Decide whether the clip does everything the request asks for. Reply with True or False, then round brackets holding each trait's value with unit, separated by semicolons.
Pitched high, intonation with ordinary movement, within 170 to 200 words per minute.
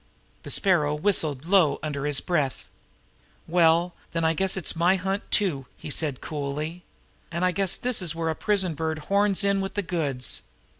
False (170 Hz; 4.1 semitones; 180 wpm)